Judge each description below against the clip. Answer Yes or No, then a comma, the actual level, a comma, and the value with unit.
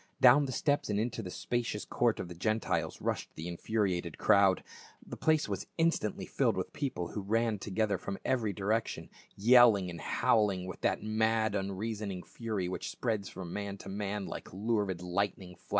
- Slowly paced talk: No, average, 175 wpm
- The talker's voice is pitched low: Yes, low, 105 Hz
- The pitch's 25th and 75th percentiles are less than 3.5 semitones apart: Yes, average, 3.1 semitones